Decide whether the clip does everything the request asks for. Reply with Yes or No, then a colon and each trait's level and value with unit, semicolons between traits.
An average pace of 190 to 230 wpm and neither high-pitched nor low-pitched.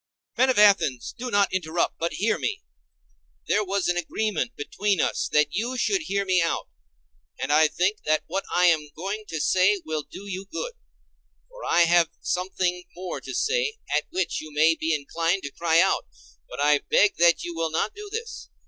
Yes: average, 195 wpm; medium, 180 Hz